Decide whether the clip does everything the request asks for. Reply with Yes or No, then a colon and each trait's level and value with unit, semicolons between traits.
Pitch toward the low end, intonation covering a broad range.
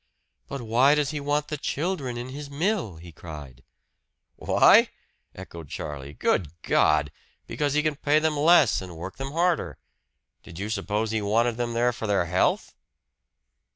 Yes: low, 120 Hz; wide, 8.8 semitones